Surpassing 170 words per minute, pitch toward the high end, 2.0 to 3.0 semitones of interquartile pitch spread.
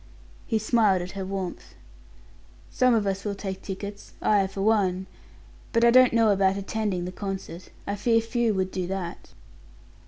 No: average, 165 wpm; high, 200 Hz; narrow, 2.6 semitones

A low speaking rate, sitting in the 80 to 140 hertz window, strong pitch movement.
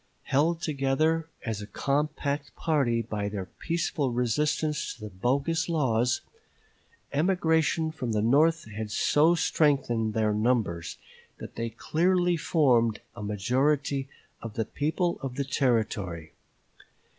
Yes: slow, 120 wpm; low, 135 Hz; wide, 5.8 semitones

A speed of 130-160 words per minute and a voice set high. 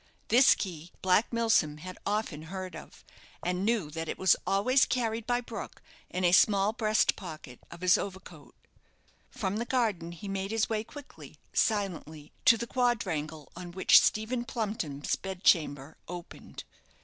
Yes: average, 155 wpm; high, 195 Hz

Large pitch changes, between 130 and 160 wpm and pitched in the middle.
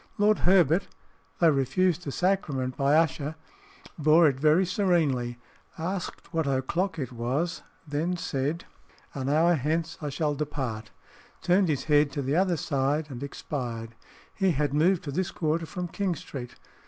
No: average, 4.2 semitones; average, 155 wpm; medium, 155 Hz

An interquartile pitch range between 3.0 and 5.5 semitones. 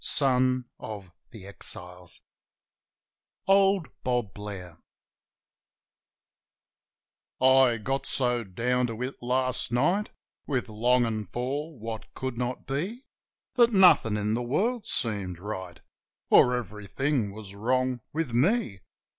Yes: average, 4.0 semitones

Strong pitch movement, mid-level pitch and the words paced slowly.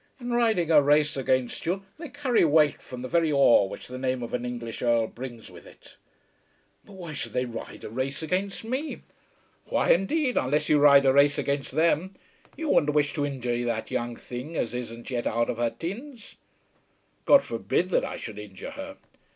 No: wide, 7.0 semitones; medium, 145 Hz; average, 190 wpm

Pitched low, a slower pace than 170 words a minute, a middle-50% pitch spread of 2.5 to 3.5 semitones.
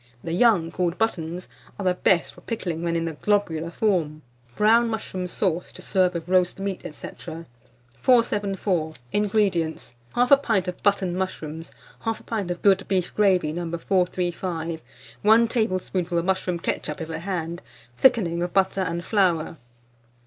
No: medium, 180 Hz; average, 150 wpm; average, 3.1 semitones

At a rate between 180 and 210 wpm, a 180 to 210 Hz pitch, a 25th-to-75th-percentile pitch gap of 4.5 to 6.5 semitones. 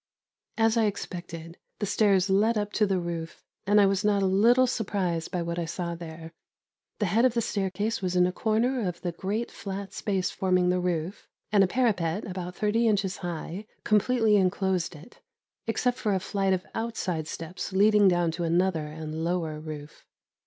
No: average, 185 wpm; high, 190 Hz; average, 3.4 semitones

